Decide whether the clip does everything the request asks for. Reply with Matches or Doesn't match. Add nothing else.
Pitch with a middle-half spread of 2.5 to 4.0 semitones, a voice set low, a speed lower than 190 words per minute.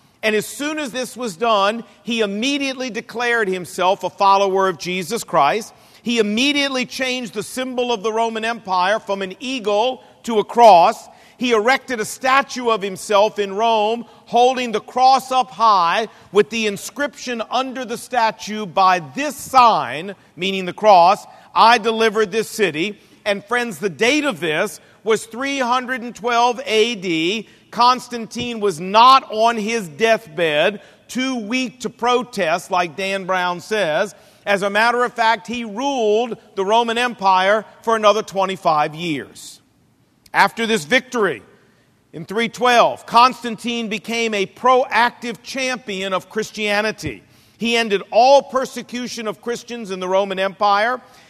Doesn't match